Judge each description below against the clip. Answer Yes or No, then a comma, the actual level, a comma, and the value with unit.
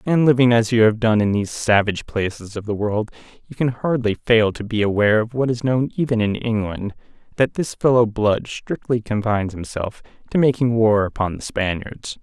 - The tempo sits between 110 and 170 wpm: No, average, 195 wpm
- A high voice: No, low, 110 Hz